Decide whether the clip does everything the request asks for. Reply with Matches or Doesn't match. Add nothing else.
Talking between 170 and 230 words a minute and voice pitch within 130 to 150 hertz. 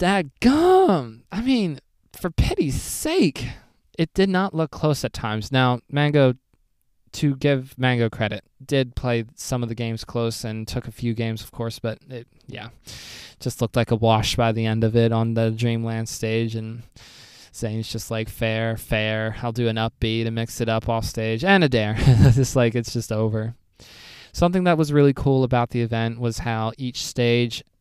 Doesn't match